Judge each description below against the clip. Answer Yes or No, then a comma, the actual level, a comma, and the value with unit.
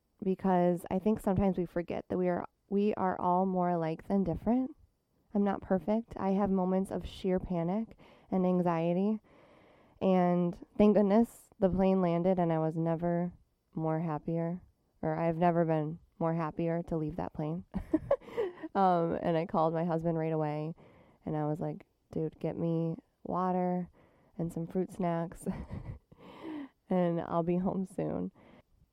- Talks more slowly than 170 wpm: Yes, average, 155 wpm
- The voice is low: No, medium, 175 Hz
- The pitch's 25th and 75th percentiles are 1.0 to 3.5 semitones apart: Yes, narrow, 2.6 semitones